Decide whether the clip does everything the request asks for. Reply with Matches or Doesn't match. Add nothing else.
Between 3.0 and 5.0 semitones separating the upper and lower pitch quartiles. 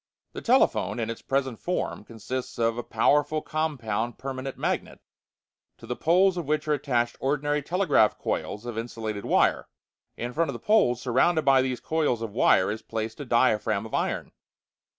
Matches